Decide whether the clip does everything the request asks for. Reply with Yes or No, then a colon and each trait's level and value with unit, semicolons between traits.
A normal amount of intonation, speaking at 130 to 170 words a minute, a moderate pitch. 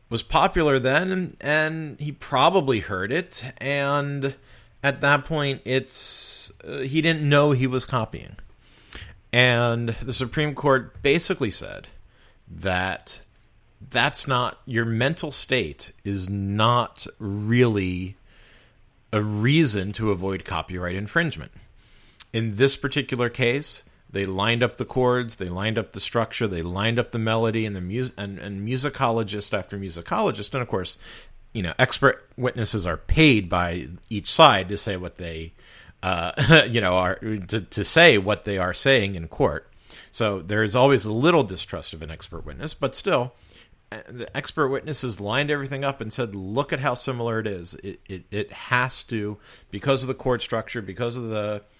No: average, 4.9 semitones; average, 160 wpm; low, 115 Hz